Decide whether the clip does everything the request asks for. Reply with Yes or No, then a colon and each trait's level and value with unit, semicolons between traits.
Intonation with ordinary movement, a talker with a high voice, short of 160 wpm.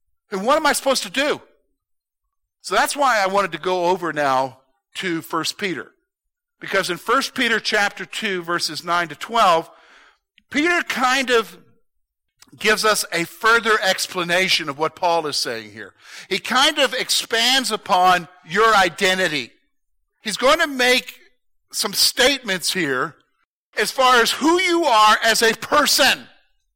No: wide, 6.7 semitones; high, 205 Hz; average, 150 wpm